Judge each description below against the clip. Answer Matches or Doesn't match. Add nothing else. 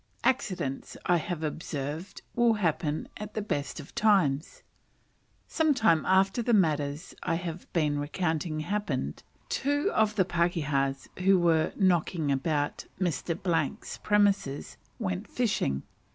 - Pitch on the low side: Doesn't match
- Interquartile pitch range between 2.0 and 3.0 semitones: Doesn't match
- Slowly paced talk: Matches